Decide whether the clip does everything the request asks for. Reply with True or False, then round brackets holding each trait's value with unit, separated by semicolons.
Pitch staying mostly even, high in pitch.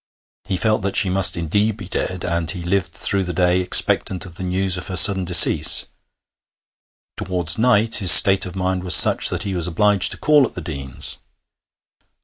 False (2.0 semitones; 95 Hz)